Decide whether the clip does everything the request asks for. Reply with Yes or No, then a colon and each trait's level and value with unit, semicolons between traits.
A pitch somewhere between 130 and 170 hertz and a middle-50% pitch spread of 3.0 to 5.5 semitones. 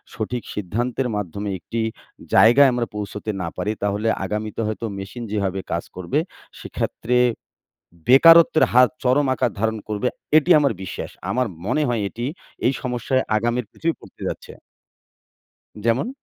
No: low, 115 Hz; average, 3.4 semitones